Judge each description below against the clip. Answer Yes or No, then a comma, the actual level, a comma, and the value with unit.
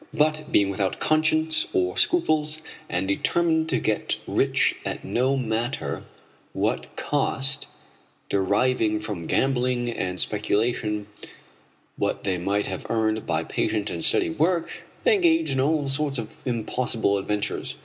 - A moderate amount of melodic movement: No, wide, 6.8 semitones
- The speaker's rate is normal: No, slow, 130 wpm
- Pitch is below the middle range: Yes, low, 120 Hz